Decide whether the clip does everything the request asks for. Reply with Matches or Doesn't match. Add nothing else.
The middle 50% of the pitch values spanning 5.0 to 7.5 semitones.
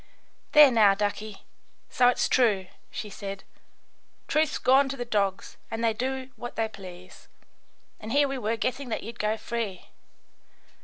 Doesn't match